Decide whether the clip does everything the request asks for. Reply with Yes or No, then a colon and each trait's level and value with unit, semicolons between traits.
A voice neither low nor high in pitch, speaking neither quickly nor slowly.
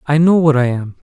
No: medium, 145 Hz; fast, 270 wpm